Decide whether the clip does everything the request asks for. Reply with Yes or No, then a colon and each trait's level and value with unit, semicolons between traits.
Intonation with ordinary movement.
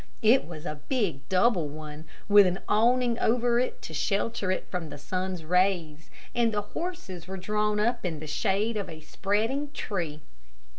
No: wide, 5.7 semitones